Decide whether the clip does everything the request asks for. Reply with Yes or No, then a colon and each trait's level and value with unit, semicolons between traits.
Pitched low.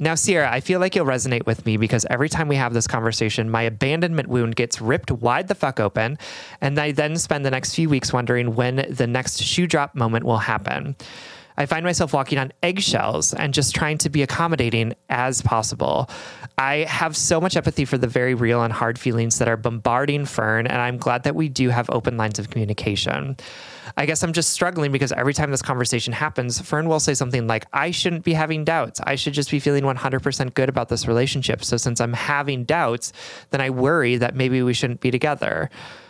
Yes: low, 130 Hz